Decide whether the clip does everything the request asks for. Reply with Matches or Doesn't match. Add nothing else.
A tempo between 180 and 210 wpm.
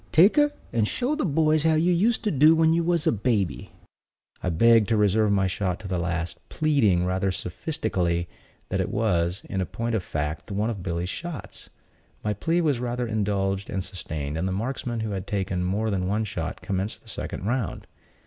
Matches